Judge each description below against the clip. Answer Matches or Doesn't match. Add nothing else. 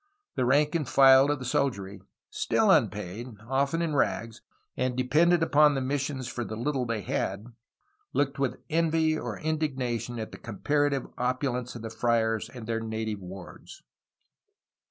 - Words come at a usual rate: Matches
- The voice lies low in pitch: Matches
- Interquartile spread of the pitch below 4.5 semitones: Matches